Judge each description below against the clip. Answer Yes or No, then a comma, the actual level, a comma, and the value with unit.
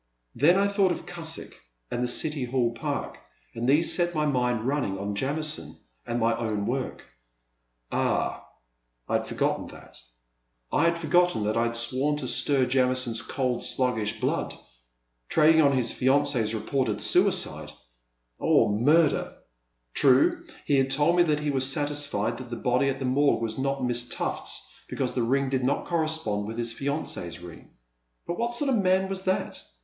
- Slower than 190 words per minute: Yes, average, 175 wpm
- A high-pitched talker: No, low, 130 Hz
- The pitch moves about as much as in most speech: Yes, average, 4.5 semitones